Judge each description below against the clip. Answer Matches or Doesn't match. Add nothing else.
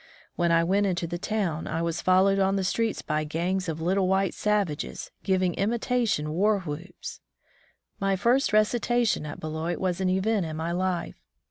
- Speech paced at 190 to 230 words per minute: Doesn't match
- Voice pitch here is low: Doesn't match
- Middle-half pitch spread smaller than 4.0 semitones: Matches